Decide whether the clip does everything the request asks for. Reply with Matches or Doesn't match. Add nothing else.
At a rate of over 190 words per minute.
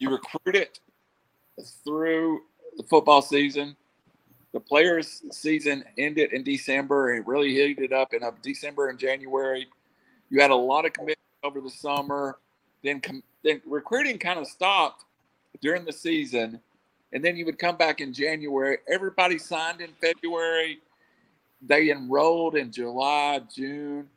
Doesn't match